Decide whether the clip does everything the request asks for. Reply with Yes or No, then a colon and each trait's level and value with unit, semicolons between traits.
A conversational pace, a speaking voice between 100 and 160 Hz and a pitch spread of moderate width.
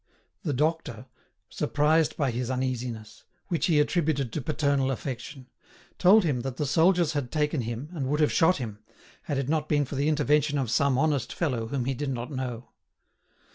Yes: average, 180 wpm; medium, 140 Hz; average, 3.4 semitones